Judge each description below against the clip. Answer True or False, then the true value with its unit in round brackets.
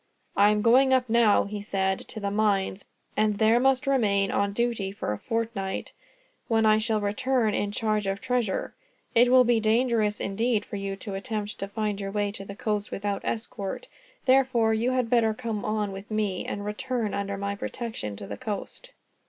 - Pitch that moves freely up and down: False (2.6 semitones)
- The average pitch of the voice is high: True (215 Hz)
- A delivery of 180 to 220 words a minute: True (190 wpm)